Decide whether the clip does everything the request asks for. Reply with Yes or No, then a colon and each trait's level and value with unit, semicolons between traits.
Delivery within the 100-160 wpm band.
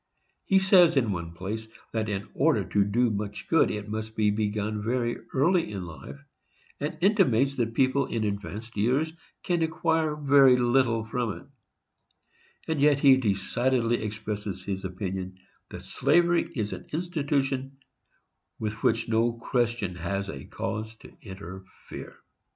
Yes: average, 140 wpm